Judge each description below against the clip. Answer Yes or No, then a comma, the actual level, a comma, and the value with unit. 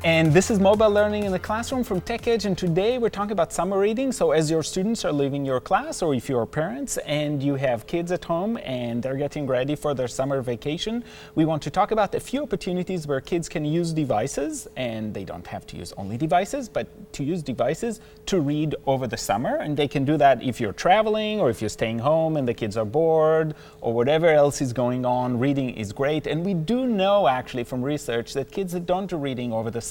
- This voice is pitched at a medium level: Yes, medium, 155 Hz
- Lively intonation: Yes, wide, 6.9 semitones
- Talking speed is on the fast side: Yes, fast, 230 wpm